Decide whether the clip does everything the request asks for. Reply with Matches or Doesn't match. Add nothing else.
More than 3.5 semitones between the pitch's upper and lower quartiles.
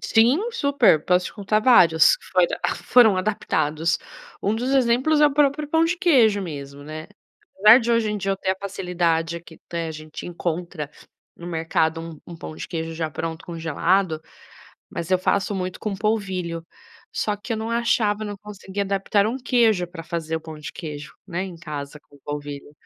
Matches